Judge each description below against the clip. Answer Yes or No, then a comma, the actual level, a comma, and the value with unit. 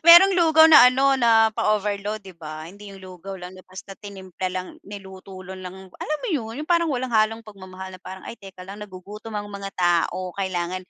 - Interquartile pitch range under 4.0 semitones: Yes, average, 3.3 semitones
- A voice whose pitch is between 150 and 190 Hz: No, high, 200 Hz